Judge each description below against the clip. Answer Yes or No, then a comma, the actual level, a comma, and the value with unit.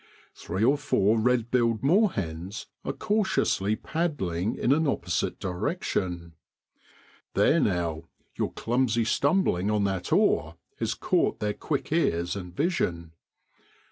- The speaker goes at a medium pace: No, slow, 120 wpm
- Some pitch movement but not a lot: No, wide, 8.0 semitones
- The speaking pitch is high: No, low, 110 Hz